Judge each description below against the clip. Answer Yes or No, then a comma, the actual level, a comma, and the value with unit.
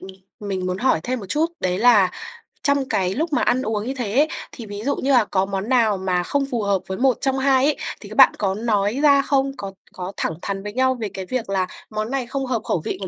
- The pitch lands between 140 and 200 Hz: No, high, 225 Hz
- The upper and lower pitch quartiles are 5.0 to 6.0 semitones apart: Yes, average, 5.3 semitones